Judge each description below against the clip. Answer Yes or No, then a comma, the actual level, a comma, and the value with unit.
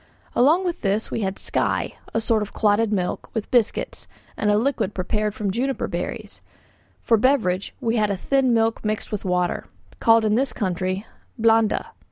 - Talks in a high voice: Yes, high, 220 Hz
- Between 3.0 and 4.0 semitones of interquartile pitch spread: No, narrow, 2.4 semitones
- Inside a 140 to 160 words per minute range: No, average, 175 wpm